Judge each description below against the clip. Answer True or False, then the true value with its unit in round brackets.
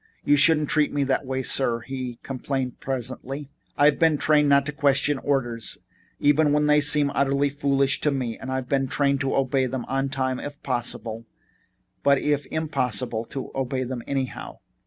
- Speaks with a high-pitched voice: False (135 Hz)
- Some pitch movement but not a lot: False (1.8 semitones)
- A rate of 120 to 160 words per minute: False (170 wpm)